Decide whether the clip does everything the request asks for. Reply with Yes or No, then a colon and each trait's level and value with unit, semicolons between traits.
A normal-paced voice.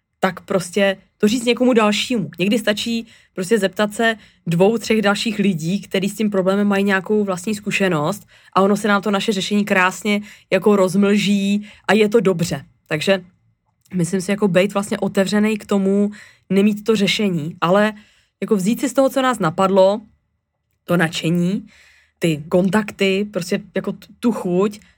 Yes: average, 160 wpm